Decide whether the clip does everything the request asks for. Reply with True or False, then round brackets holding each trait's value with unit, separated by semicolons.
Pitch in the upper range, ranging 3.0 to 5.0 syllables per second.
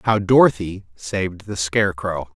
False (95 Hz; 4.7 syllables/s)